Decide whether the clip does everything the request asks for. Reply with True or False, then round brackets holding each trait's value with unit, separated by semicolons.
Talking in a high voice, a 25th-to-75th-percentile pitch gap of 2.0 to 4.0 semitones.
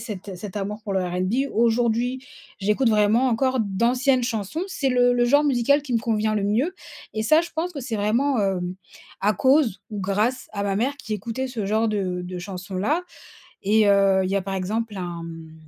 False (220 Hz; 4.4 semitones)